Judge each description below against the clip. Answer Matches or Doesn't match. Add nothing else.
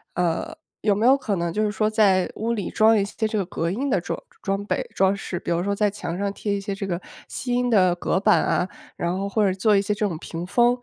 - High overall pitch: Matches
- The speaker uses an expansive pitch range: Doesn't match